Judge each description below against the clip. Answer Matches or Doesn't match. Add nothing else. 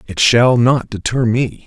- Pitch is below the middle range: Matches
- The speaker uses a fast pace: Doesn't match